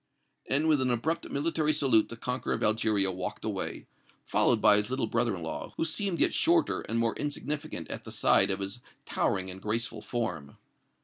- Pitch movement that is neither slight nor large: No, wide, 6.2 semitones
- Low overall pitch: Yes, low, 115 Hz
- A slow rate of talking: No, average, 190 wpm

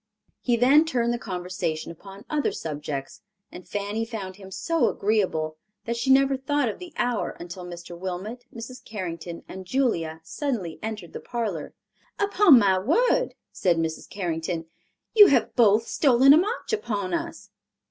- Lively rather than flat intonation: Yes, wide, 7.0 semitones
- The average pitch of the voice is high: Yes, high, 210 Hz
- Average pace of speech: Yes, average, 155 wpm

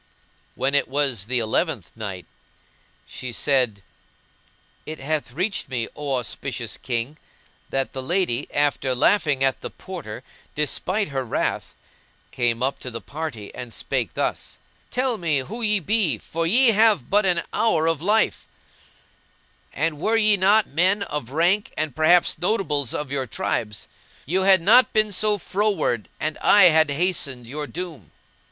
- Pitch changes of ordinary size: No, wide, 6.6 semitones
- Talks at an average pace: Yes, average, 150 wpm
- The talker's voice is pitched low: No, medium, 155 Hz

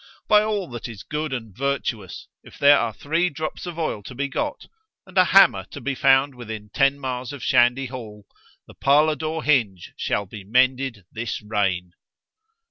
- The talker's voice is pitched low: Yes, low, 130 Hz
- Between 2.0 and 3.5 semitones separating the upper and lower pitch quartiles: No, average, 5.3 semitones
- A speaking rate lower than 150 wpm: No, average, 175 wpm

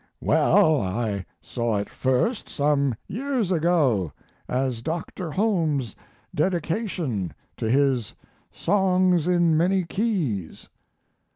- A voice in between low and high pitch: Yes, medium, 155 Hz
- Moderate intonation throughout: No, wide, 7.1 semitones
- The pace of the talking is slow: Yes, slow, 95 wpm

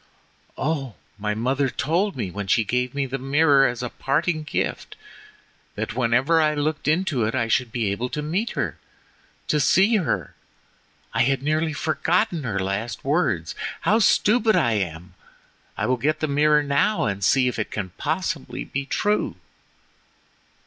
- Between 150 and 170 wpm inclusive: Yes, average, 155 wpm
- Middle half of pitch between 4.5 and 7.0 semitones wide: Yes, average, 5.0 semitones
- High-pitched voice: No, medium, 140 Hz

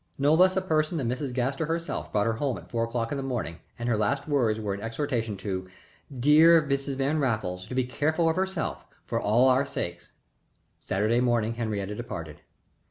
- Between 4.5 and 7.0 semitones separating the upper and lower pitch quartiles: Yes, average, 5.0 semitones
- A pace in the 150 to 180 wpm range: No, average, 200 wpm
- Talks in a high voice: No, low, 125 Hz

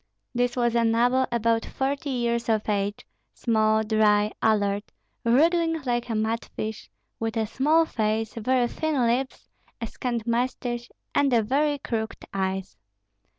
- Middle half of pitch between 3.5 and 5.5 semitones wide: No, average, 2.7 semitones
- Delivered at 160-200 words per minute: No, average, 140 wpm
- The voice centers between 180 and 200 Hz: No, high, 235 Hz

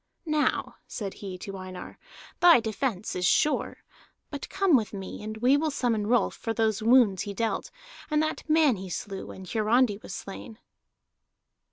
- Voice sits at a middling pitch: No, high, 220 Hz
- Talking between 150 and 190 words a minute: Yes, average, 165 wpm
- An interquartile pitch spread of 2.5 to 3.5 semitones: No, average, 5.0 semitones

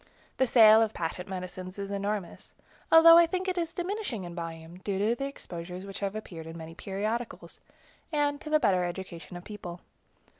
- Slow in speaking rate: No, average, 190 wpm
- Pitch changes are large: Yes, wide, 6.7 semitones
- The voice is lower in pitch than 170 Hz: No, high, 200 Hz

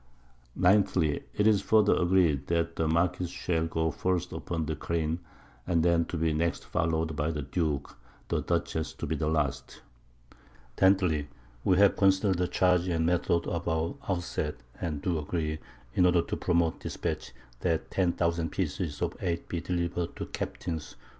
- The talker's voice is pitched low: Yes, very low, 85 Hz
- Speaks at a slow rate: No, average, 165 wpm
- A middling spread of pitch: No, narrow, 2.1 semitones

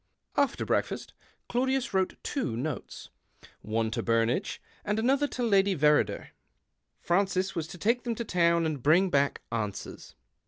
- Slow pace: No, average, 155 wpm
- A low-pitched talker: No, medium, 180 Hz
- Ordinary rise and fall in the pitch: No, wide, 8.2 semitones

